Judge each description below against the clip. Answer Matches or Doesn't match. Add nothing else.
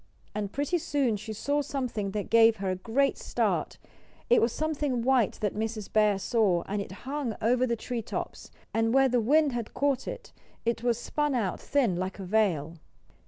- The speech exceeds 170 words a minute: Matches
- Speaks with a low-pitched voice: Doesn't match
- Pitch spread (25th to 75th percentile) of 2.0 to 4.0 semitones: Doesn't match